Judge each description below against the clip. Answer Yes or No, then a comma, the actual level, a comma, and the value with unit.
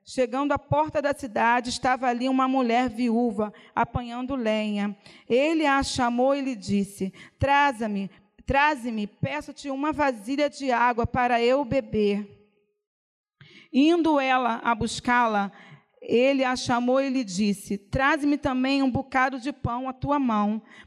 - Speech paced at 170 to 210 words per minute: No, average, 130 wpm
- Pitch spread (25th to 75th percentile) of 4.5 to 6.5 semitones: No, average, 4.1 semitones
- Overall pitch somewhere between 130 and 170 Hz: No, very high, 255 Hz